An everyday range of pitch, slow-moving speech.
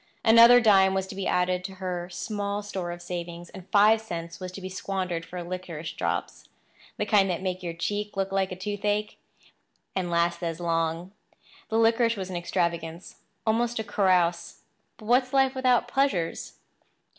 No: average, 3.3 semitones; average, 165 wpm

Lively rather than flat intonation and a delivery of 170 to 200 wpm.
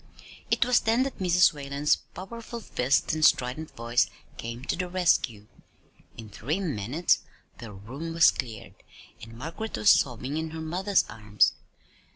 No: wide, 7.4 semitones; average, 150 wpm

